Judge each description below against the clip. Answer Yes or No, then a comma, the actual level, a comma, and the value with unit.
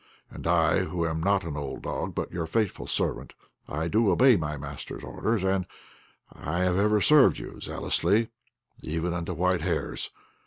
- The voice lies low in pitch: Yes, very low, 90 Hz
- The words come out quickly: No, average, 165 wpm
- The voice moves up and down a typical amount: Yes, average, 3.5 semitones